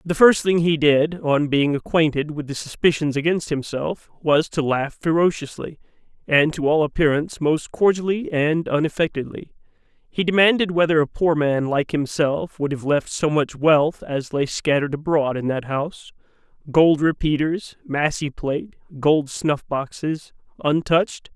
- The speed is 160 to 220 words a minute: No, average, 145 wpm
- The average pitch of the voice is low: No, medium, 155 Hz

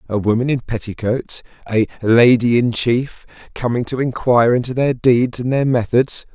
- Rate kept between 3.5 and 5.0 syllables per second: Yes, 4.7 syllables/s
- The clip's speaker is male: Yes, male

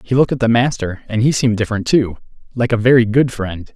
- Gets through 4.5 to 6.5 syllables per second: No, 6.8 syllables/s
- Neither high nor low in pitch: No, low, 115 Hz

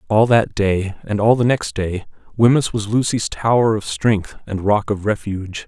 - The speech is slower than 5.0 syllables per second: Yes, 4.6 syllables/s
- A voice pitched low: Yes, low, 105 Hz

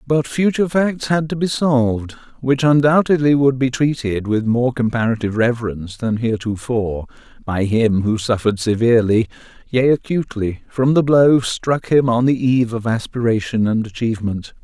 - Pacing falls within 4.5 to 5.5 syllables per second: Yes, 5.2 syllables/s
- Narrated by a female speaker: No, male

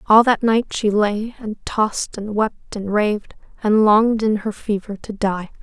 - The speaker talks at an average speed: Yes, average, 190 wpm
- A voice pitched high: Yes, high, 215 Hz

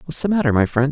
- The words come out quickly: Yes, fast, 330 wpm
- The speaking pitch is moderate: Yes, medium, 145 Hz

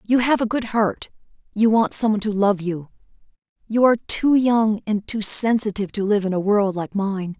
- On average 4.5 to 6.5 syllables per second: Yes, 5.1 syllables/s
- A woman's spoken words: Yes, female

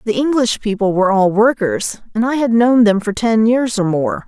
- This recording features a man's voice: No, female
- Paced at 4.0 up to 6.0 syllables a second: Yes, 5.0 syllables/s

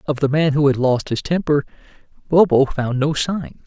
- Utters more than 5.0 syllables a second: No, 4.9 syllables/s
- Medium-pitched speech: Yes, medium, 145 Hz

